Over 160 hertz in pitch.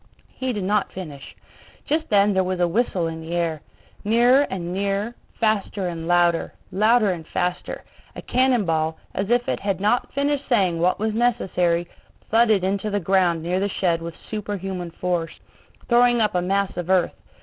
Yes: high, 190 Hz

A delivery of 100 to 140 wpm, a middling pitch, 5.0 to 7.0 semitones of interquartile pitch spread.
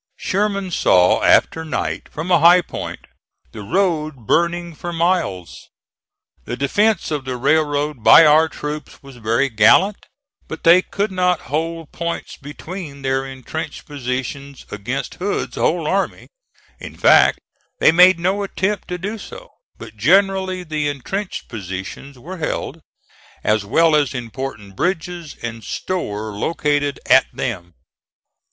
Yes: slow, 135 wpm; medium, 155 Hz; wide, 5.4 semitones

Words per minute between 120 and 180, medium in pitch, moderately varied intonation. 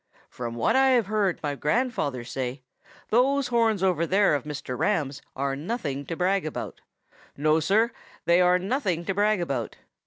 No: average, 165 wpm; medium, 180 Hz; wide, 7.0 semitones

